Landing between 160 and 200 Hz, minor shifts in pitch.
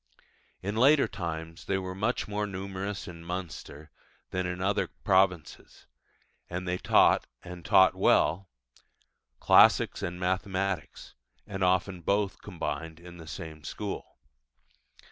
No: very low, 95 Hz; narrow, 2.2 semitones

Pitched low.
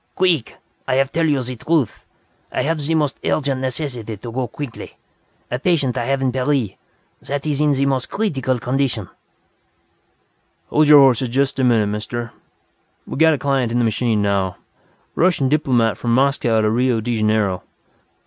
Yes: low, 130 Hz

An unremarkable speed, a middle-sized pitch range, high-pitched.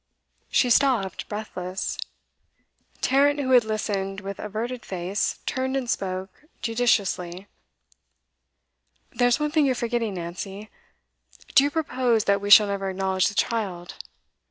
No: slow, 125 wpm; average, 4.5 semitones; high, 215 Hz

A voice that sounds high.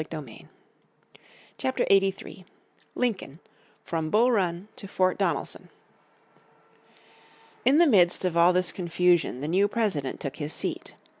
No: medium, 180 Hz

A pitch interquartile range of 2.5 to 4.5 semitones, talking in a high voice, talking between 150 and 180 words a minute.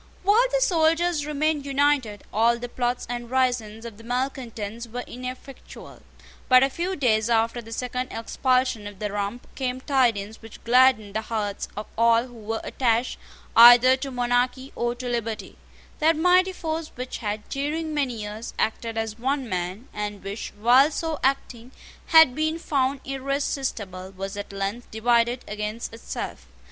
Yes: average, 3.6 semitones; high, 245 Hz; average, 155 wpm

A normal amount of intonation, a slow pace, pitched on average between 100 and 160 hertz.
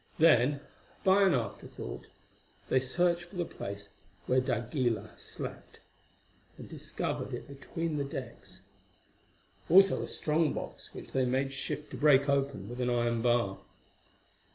Yes: average, 4.2 semitones; slow, 130 wpm; low, 135 Hz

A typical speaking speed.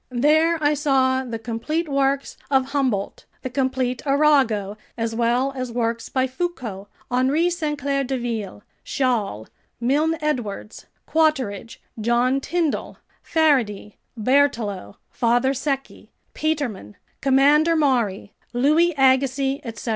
No: slow, 110 wpm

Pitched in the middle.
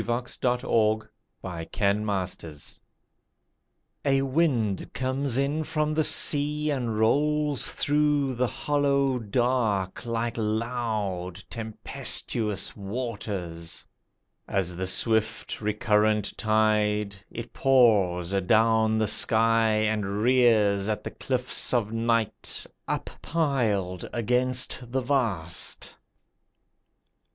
No: low, 115 Hz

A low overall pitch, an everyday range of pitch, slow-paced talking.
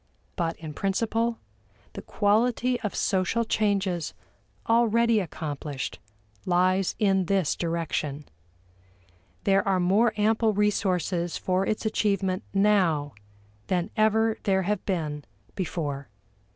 No: high, 195 Hz; average, 3.8 semitones; slow, 105 wpm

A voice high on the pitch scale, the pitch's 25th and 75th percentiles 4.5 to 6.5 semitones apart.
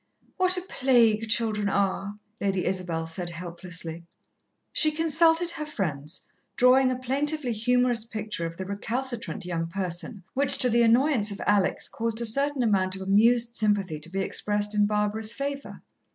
Yes: high, 215 Hz; average, 4.9 semitones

